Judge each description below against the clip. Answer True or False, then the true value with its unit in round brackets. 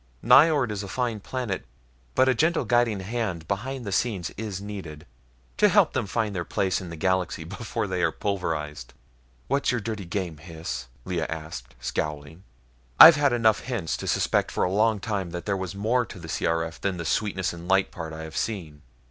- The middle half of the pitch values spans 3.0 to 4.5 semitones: False (5.4 semitones)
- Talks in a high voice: False (95 Hz)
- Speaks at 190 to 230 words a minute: True (195 wpm)